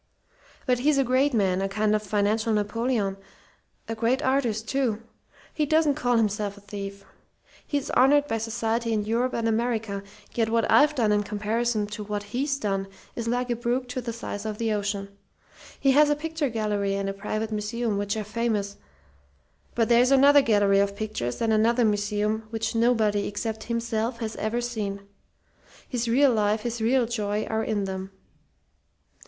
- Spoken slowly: No, average, 175 wpm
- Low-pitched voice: No, high, 225 Hz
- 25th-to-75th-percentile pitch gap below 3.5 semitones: Yes, average, 2.7 semitones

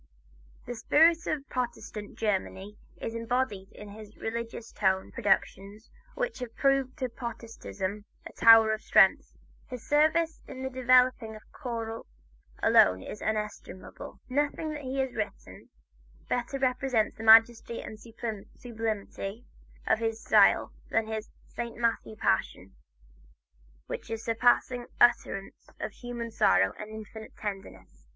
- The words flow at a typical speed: No, slow, 125 wpm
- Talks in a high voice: Yes, high, 225 Hz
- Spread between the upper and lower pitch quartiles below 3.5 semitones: Yes, average, 3.0 semitones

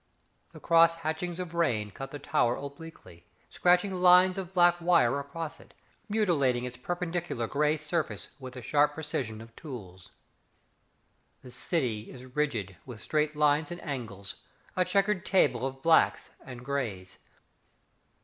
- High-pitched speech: No, medium, 150 Hz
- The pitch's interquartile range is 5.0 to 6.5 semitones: Yes, wide, 5.5 semitones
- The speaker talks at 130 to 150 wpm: Yes, average, 140 wpm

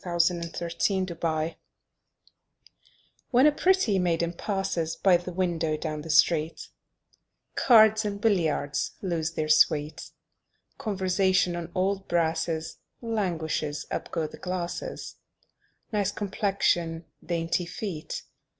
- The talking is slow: Yes, slow, 115 wpm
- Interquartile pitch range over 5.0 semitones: No, average, 3.1 semitones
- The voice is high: No, medium, 175 Hz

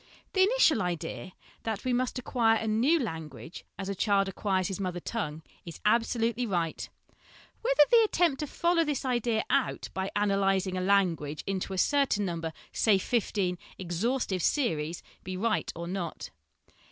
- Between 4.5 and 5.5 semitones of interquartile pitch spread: Yes, average, 5.2 semitones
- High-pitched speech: Yes, high, 200 Hz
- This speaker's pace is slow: No, average, 165 wpm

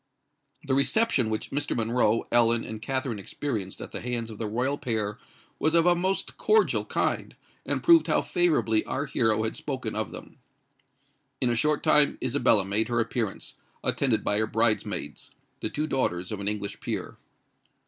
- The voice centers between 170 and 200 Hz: No, low, 115 Hz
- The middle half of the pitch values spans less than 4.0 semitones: No, average, 4.5 semitones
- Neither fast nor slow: Yes, average, 170 wpm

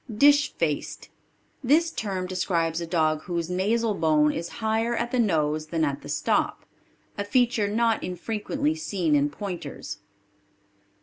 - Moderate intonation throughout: No, wide, 6.2 semitones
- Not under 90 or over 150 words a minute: Yes, average, 140 wpm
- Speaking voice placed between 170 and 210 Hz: Yes, high, 190 Hz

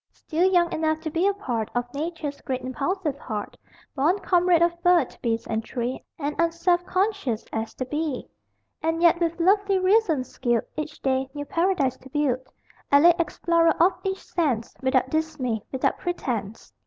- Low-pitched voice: No, very high, 315 Hz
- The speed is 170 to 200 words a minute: No, average, 160 wpm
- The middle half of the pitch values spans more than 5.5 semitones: No, average, 5.1 semitones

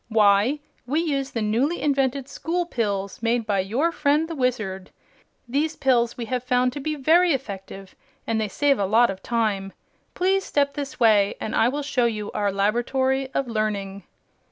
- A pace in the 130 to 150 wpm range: No, average, 180 wpm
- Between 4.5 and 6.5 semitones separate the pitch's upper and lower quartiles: Yes, average, 5.1 semitones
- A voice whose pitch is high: Yes, high, 245 Hz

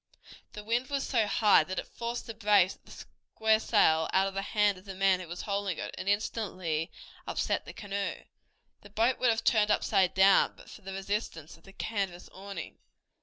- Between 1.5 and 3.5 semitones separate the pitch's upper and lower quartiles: Yes, narrow, 2.5 semitones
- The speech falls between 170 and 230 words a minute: Yes, fast, 205 wpm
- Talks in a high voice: Yes, high, 200 Hz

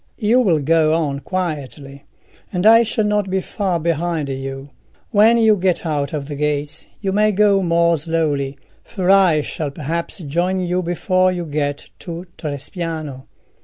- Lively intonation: No, average, 4.3 semitones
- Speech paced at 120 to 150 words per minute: No, average, 160 wpm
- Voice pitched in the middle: Yes, medium, 170 Hz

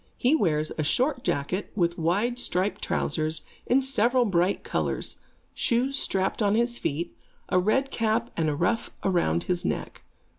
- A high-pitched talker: Yes, high, 200 Hz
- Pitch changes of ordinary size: No, wide, 6.0 semitones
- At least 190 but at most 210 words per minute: No, average, 155 wpm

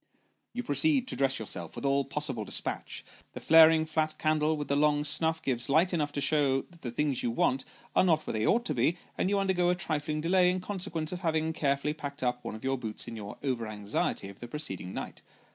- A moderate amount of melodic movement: Yes, average, 3.9 semitones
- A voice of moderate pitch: Yes, medium, 150 Hz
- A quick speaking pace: Yes, fast, 230 wpm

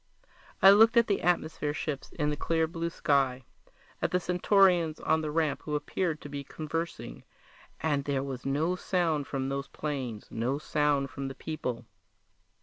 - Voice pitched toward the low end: No, medium, 150 Hz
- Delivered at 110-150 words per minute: No, average, 165 wpm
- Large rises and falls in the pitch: No, average, 3.3 semitones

